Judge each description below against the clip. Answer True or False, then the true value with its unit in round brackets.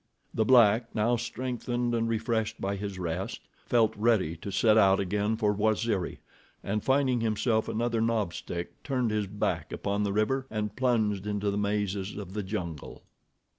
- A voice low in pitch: True (105 Hz)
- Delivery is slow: False (165 wpm)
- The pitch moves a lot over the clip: False (2.4 semitones)